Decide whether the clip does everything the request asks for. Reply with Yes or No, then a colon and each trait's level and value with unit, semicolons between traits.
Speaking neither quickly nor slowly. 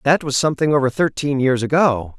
Yes: average, 190 wpm